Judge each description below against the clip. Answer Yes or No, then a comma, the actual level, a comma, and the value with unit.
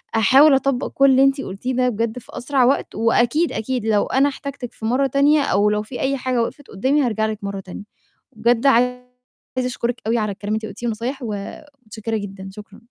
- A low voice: No, high, 240 Hz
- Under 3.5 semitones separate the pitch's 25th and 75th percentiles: No, average, 3.8 semitones